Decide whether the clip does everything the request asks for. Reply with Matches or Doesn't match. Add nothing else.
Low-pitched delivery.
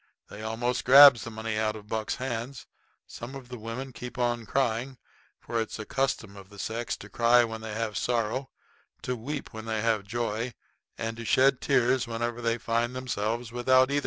Matches